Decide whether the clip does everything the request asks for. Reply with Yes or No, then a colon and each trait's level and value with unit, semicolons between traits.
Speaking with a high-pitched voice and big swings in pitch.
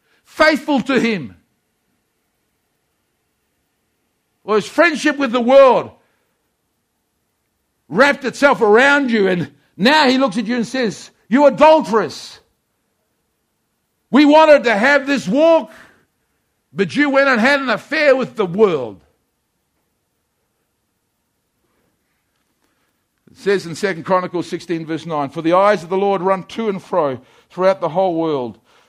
Yes: high, 220 Hz; wide, 7.0 semitones